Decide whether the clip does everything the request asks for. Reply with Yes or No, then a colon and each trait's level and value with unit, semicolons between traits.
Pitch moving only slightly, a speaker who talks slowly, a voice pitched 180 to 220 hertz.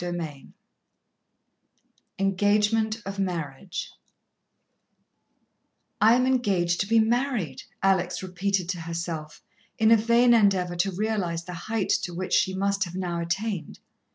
No: average, 3.8 semitones; slow, 125 wpm; high, 190 Hz